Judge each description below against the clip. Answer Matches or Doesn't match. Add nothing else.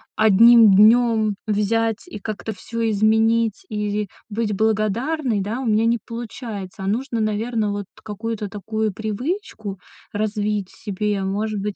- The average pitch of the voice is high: Matches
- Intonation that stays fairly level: Matches